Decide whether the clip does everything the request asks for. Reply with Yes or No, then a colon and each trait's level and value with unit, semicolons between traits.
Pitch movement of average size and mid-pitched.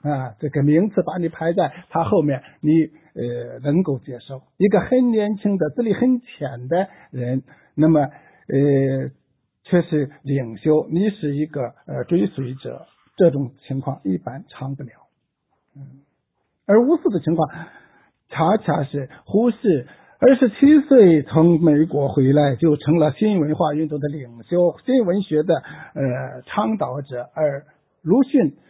Yes: average, 4.7 semitones; medium, 155 Hz